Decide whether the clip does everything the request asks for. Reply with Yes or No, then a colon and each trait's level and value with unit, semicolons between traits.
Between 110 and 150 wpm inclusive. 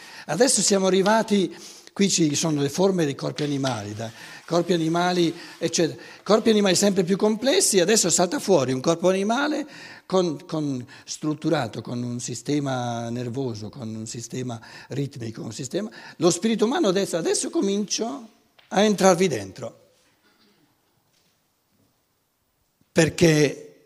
Yes: average, 125 wpm